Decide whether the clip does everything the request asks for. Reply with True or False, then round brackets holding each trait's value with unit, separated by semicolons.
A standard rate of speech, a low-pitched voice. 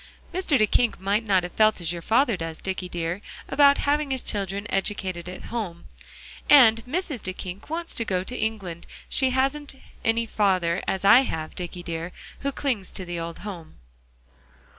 False (170 wpm; 200 Hz)